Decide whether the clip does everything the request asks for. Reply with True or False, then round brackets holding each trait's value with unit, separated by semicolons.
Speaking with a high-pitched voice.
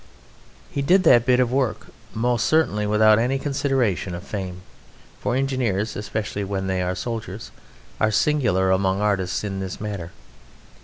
False (105 Hz)